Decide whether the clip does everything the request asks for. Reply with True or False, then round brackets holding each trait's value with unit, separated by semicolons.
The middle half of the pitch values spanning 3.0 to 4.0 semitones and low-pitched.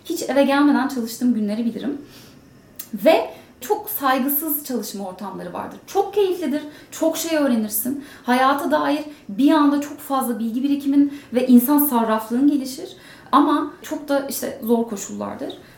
False (3.6 semitones; 280 Hz)